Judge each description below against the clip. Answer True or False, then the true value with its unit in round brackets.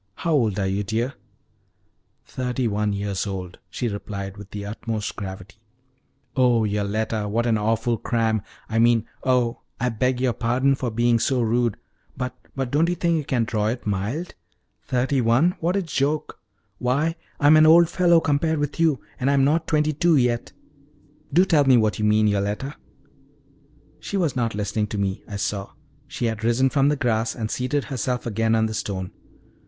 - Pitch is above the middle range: False (120 Hz)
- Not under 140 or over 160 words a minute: False (180 wpm)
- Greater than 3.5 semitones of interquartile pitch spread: True (4.6 semitones)